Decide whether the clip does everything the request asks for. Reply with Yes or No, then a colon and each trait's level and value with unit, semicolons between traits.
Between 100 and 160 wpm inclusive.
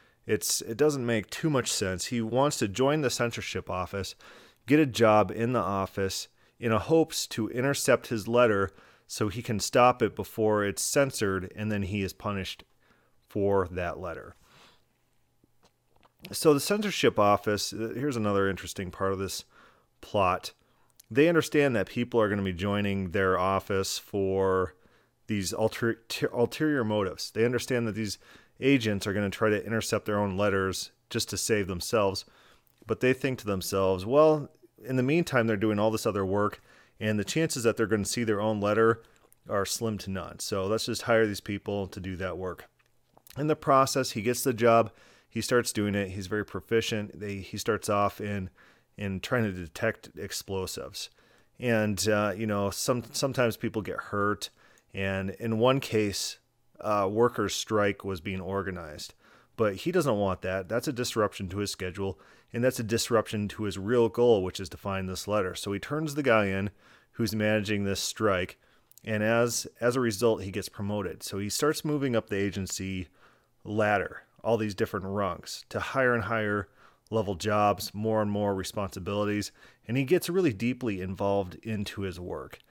No: average, 180 wpm